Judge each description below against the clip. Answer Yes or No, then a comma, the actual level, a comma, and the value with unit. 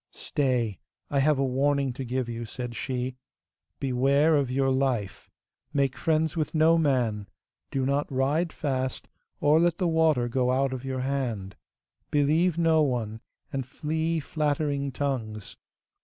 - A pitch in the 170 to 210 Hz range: No, low, 135 Hz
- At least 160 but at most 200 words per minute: No, average, 145 wpm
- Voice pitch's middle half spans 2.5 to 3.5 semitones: Yes, average, 3.1 semitones